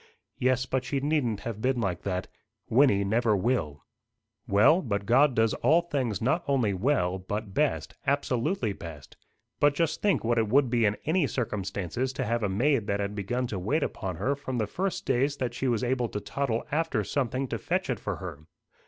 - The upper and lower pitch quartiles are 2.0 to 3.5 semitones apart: No, average, 5.3 semitones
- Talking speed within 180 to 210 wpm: Yes, average, 195 wpm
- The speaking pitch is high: No, low, 120 Hz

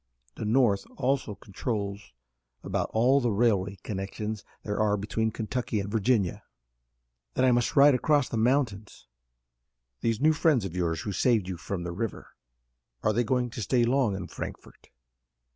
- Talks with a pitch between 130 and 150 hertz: No, low, 110 Hz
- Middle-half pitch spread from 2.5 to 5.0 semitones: Yes, average, 3.9 semitones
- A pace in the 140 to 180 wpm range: Yes, average, 160 wpm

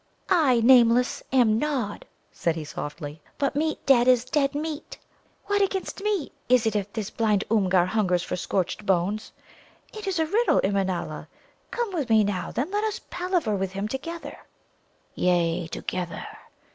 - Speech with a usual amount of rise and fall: No, wide, 8.2 semitones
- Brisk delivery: No, average, 160 wpm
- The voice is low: No, high, 230 Hz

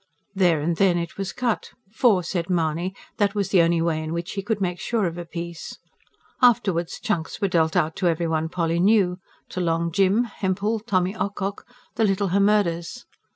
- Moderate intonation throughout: Yes, average, 3.1 semitones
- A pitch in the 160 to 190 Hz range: Yes, medium, 185 Hz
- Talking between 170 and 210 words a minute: Yes, average, 190 wpm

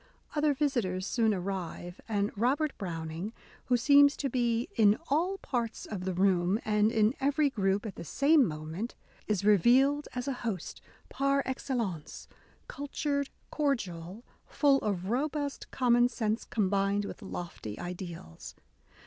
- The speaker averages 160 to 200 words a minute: No, average, 140 wpm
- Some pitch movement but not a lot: No, wide, 6.4 semitones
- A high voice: Yes, high, 225 Hz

